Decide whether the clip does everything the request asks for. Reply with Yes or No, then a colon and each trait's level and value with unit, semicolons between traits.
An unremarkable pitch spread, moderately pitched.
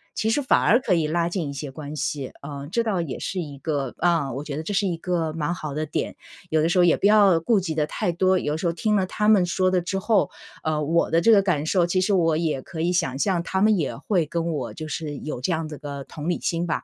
Yes: average, 3.5 semitones; medium, 170 Hz